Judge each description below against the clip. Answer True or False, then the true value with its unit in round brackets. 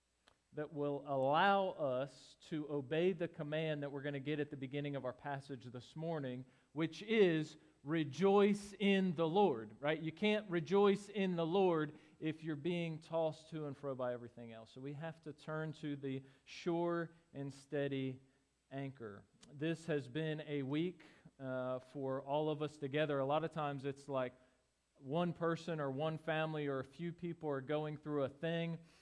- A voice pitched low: False (150 Hz)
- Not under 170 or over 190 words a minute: True (180 wpm)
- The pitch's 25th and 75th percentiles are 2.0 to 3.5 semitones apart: True (3.2 semitones)